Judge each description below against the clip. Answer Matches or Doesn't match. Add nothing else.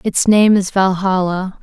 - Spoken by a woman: Matches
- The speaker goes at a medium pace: Matches